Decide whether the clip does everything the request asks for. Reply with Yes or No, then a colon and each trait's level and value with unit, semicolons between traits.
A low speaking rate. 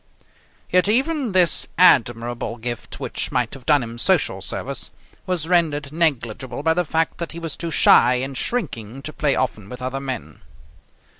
No: average, 165 wpm